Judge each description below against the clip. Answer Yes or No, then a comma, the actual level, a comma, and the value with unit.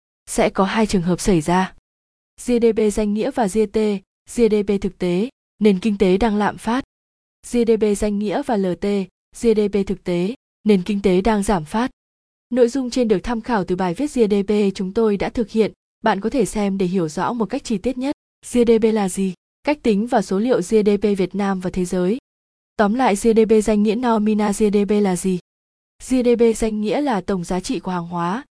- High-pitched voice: Yes, high, 210 Hz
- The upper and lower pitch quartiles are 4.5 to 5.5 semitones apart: No, average, 2.9 semitones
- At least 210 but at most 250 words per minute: No, average, 200 wpm